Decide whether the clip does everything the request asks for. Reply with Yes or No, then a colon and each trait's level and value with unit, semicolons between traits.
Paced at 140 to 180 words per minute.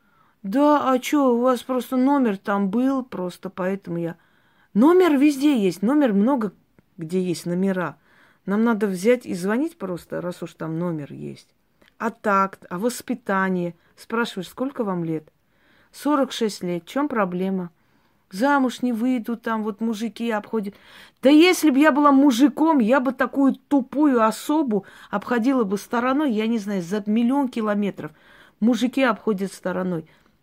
Yes: average, 145 wpm